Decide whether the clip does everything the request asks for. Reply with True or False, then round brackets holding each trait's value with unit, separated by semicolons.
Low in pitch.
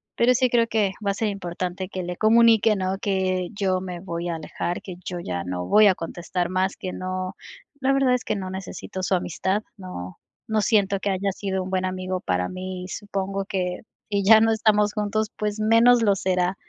False (190 Hz)